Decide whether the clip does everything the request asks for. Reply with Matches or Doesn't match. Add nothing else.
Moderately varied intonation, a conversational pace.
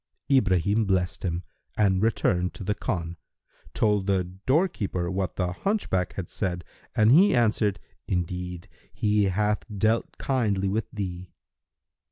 Doesn't match